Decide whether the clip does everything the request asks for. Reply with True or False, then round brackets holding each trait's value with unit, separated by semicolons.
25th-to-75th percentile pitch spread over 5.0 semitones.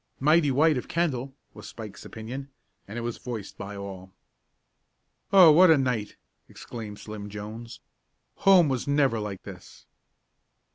True (5.6 semitones)